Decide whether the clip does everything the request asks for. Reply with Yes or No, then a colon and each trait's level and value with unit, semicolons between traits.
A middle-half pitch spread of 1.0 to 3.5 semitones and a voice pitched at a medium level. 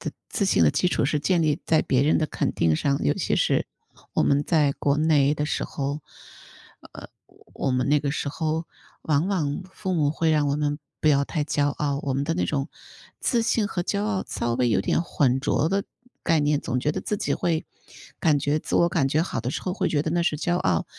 Yes: average, 2.8 semitones; medium, 150 Hz